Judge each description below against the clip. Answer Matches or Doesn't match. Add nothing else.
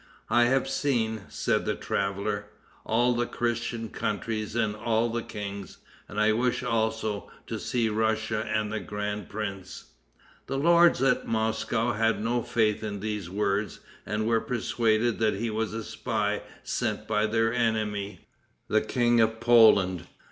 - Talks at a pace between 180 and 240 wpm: Doesn't match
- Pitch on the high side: Doesn't match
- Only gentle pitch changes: Matches